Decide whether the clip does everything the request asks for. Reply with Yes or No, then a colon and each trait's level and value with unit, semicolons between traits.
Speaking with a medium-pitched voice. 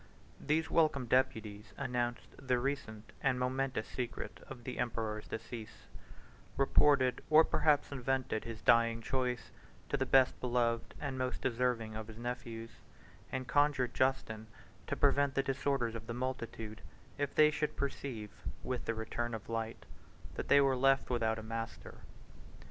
No: low, 125 Hz